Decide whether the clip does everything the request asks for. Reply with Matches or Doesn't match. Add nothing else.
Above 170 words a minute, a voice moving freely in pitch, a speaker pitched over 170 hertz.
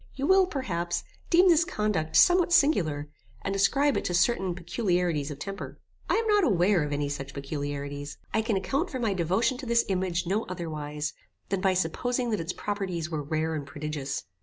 Matches